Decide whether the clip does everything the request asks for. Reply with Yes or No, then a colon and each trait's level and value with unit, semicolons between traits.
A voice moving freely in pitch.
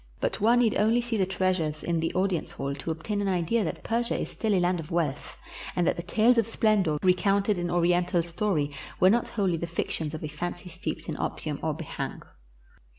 No: average, 3.9 semitones